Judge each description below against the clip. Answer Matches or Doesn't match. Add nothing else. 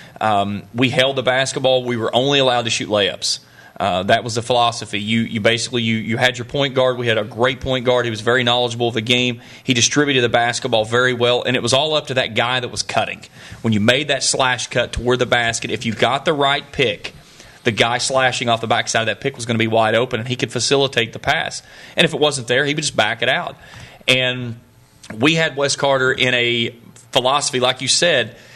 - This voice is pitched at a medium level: Doesn't match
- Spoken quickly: Matches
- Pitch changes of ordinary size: Doesn't match